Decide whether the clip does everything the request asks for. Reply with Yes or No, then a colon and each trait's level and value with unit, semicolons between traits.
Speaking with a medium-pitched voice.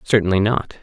No: low, 100 Hz